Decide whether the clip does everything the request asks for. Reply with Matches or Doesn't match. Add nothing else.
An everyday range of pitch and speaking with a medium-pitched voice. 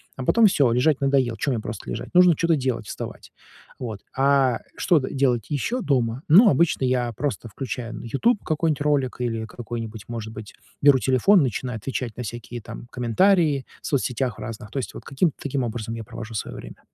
Doesn't match